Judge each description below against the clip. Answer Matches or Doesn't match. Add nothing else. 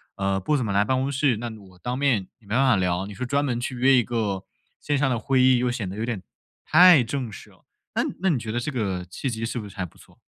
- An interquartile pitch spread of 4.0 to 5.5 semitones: Matches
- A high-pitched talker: Doesn't match